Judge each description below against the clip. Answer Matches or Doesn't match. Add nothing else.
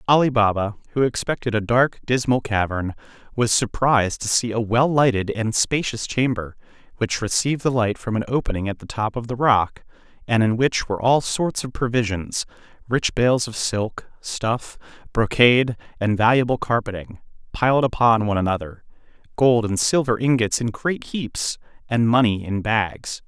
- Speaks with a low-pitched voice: Matches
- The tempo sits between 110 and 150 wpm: Doesn't match